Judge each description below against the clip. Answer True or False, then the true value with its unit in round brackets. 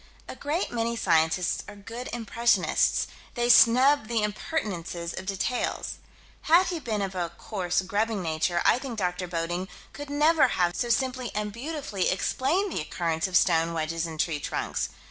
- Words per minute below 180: True (165 wpm)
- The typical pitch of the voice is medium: False (210 Hz)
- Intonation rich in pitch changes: True (6.1 semitones)